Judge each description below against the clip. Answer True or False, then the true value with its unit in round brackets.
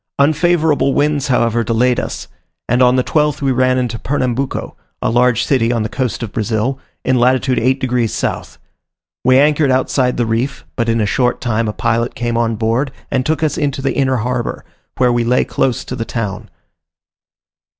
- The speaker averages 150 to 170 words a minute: False (185 wpm)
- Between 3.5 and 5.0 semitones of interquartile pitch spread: False (2.4 semitones)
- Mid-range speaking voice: False (125 Hz)